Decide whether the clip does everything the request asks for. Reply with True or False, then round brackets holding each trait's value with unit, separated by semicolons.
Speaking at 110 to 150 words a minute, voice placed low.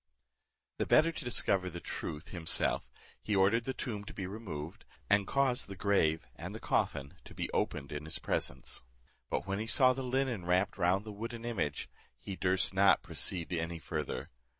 False (180 wpm; 95 Hz)